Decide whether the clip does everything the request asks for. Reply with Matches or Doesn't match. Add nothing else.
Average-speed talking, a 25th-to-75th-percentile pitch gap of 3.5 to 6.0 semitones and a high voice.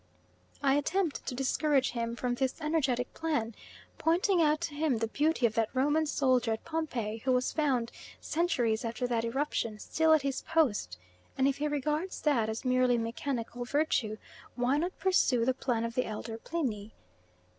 Matches